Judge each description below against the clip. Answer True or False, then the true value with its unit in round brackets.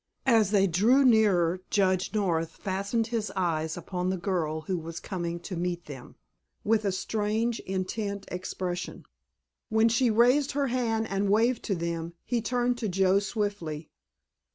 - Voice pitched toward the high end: True (195 Hz)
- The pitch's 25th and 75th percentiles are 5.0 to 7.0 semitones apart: False (4.2 semitones)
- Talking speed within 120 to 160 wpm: True (155 wpm)